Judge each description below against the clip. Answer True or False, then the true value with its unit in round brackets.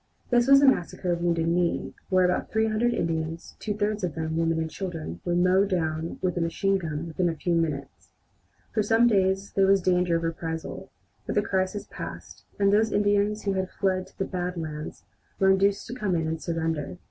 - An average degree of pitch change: True (3.4 semitones)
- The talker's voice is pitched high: False (180 Hz)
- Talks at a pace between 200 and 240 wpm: True (205 wpm)